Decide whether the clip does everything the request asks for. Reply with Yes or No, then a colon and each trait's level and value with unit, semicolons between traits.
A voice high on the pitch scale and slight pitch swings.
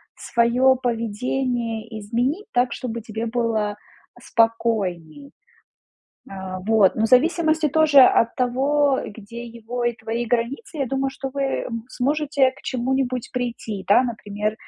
No: high, 240 Hz; average, 3.1 semitones